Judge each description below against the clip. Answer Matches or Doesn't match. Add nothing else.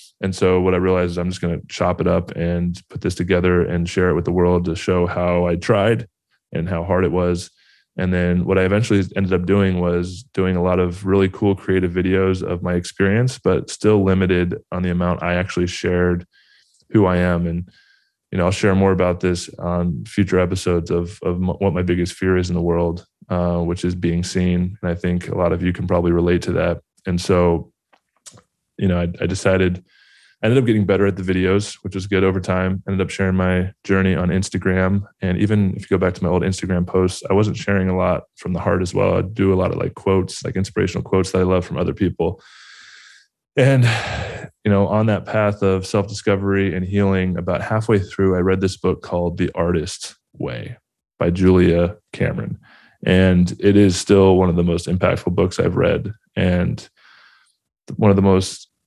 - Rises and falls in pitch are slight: Matches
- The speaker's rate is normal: Doesn't match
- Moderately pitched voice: Doesn't match